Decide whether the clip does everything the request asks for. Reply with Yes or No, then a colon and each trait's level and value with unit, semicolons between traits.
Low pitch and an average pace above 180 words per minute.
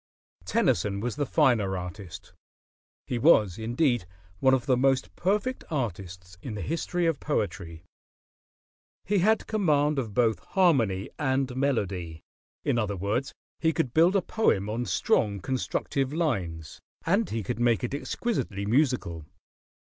No: low, 120 Hz; average, 140 wpm